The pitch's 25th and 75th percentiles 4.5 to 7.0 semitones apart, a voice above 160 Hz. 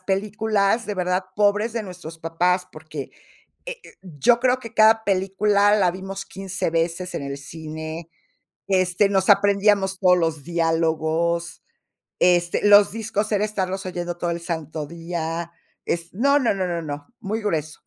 No: average, 3.6 semitones; medium, 185 Hz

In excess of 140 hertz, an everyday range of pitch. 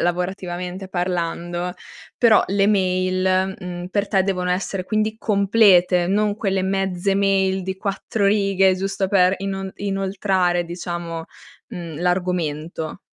No: high, 190 Hz; narrow, 1.7 semitones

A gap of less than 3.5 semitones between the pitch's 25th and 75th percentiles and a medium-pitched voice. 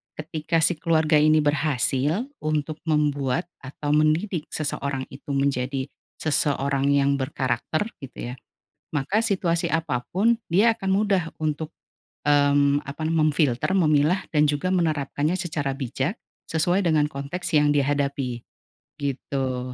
Yes: average, 2.8 semitones; medium, 150 Hz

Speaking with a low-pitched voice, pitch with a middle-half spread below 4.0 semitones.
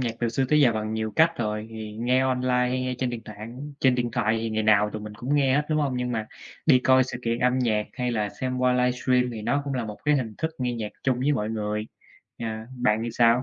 Yes: low, 120 Hz; average, 2.7 semitones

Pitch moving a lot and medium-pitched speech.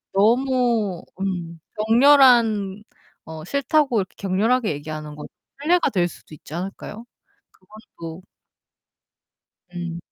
No: wide, 5.9 semitones; high, 200 Hz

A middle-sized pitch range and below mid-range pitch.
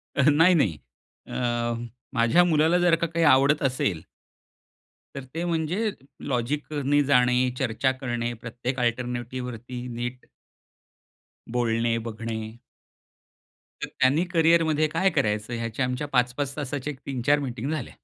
Yes: average, 4.0 semitones; low, 130 Hz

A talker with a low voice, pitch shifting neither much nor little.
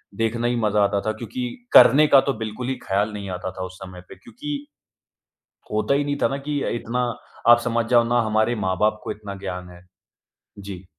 Yes: low, 110 Hz; average, 3.6 semitones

